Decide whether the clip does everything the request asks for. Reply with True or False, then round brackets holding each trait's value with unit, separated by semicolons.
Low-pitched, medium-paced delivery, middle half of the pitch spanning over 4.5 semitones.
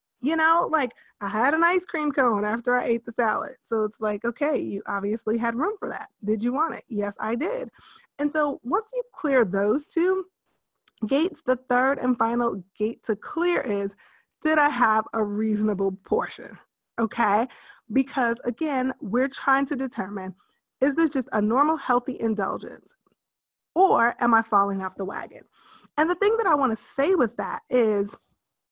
False (245 Hz; 180 wpm; 5.6 semitones)